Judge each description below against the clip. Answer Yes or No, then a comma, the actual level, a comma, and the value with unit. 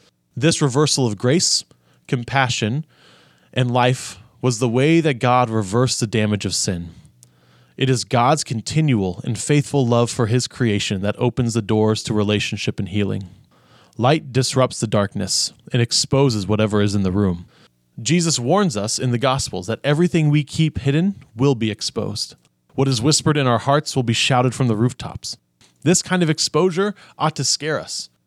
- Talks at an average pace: Yes, average, 170 wpm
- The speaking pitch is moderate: No, low, 125 Hz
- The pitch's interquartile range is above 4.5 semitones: Yes, average, 4.9 semitones